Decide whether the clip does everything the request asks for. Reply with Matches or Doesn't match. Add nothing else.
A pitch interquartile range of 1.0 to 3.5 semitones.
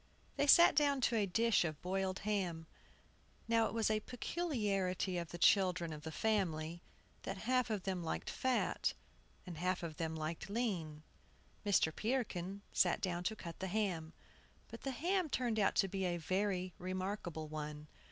Doesn't match